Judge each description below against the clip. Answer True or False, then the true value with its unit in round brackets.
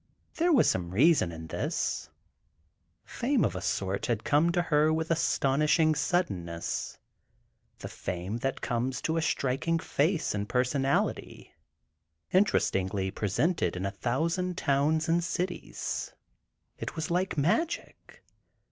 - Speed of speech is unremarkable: False (120 wpm)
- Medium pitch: True (150 Hz)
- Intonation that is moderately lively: False (8.4 semitones)